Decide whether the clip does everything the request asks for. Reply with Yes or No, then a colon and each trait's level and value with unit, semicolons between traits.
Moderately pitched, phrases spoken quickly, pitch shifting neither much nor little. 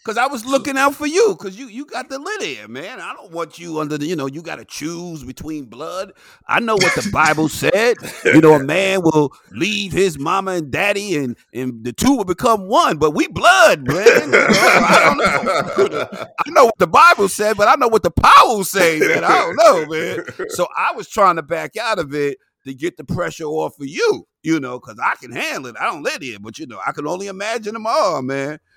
No: medium, 180 Hz; fast, 240 wpm; wide, 7.6 semitones